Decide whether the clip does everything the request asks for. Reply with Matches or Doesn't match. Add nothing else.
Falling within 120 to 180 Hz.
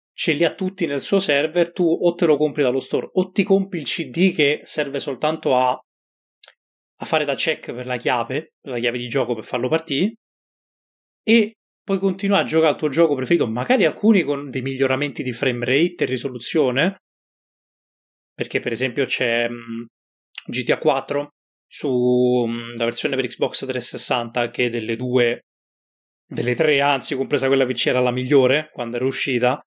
Matches